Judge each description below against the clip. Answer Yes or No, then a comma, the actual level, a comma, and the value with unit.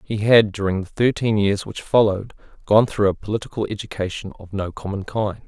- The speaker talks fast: No, average, 185 wpm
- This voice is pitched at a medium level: No, low, 100 Hz